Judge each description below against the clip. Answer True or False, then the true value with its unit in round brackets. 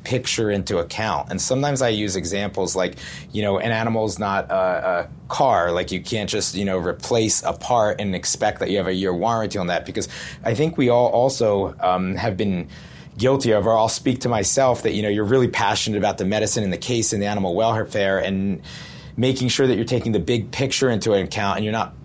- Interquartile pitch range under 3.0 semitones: False (3.6 semitones)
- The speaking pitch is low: True (110 Hz)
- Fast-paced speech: True (225 wpm)